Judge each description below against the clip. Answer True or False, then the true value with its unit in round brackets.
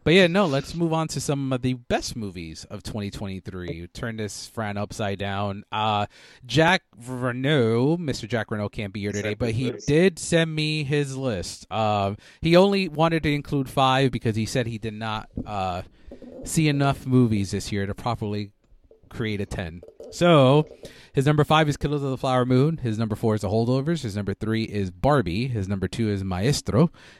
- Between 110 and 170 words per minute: False (195 wpm)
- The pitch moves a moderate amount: False (5.8 semitones)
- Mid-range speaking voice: False (120 Hz)